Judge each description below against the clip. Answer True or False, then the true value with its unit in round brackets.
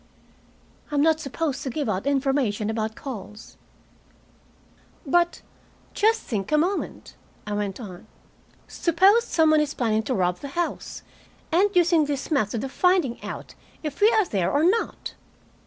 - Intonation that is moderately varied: False (7.4 semitones)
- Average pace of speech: True (150 wpm)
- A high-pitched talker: True (285 Hz)